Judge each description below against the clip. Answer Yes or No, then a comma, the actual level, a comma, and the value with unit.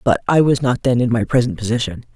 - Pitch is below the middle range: Yes, low, 120 Hz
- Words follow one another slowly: No, fast, 250 wpm